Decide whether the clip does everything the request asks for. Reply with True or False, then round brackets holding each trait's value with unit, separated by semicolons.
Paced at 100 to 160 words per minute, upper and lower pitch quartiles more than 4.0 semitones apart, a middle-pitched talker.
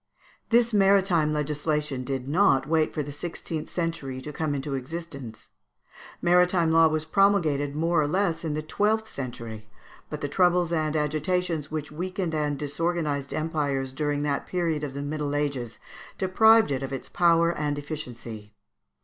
False (155 wpm; 3.2 semitones; 155 Hz)